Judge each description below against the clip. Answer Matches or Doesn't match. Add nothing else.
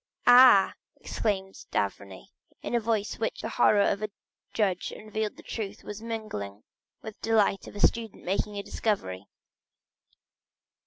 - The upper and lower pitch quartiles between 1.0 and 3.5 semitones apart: Matches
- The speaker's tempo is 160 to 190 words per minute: Doesn't match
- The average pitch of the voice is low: Doesn't match